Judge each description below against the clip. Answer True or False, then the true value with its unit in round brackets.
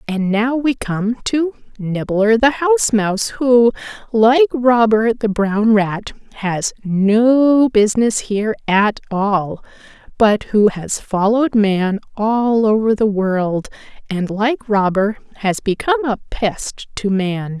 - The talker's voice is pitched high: True (220 Hz)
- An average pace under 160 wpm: True (135 wpm)